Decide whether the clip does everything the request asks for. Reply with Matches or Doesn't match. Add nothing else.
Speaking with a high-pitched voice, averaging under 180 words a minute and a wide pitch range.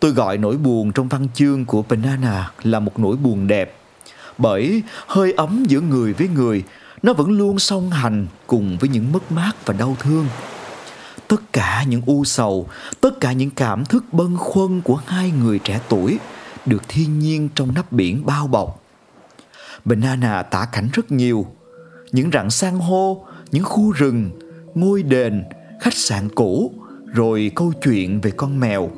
Doesn't match